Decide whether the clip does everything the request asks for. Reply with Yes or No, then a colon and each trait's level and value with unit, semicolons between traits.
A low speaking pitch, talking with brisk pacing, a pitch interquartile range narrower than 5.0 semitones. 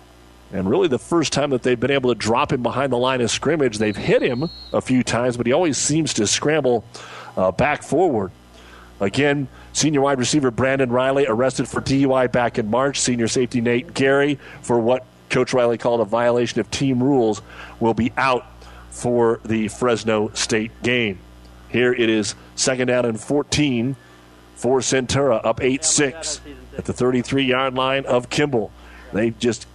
No: low, 120 Hz; average, 175 wpm; average, 3.3 semitones